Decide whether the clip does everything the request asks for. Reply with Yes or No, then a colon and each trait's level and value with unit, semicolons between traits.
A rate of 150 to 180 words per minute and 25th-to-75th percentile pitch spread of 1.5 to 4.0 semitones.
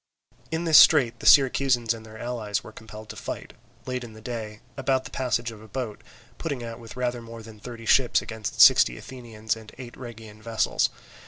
No: average, 195 wpm; narrow, 2.4 semitones